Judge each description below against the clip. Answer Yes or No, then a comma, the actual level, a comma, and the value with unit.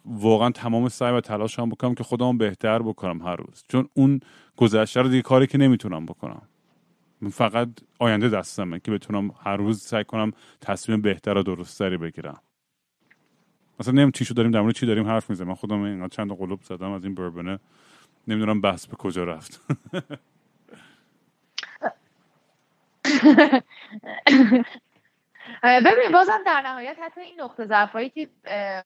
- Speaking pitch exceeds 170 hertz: No, low, 120 Hz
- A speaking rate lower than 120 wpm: No, average, 145 wpm